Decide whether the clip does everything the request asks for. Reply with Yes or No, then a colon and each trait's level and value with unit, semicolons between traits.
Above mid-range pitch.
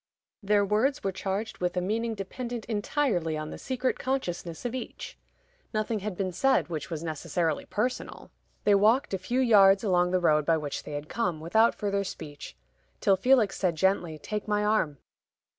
Yes: high, 195 Hz